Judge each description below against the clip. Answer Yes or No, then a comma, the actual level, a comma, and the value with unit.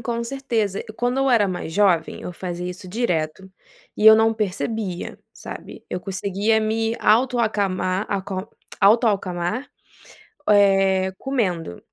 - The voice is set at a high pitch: Yes, high, 200 Hz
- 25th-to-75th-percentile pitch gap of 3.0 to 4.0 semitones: Yes, average, 3.3 semitones